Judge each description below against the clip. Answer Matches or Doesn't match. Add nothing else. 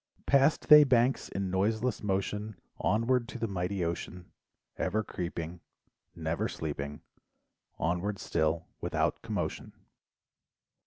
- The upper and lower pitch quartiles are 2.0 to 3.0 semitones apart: Doesn't match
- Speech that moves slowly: Matches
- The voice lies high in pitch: Doesn't match